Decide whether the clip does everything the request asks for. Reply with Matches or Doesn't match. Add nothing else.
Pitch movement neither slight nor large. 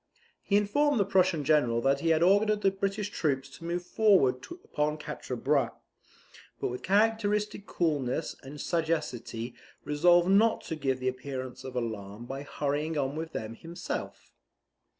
Doesn't match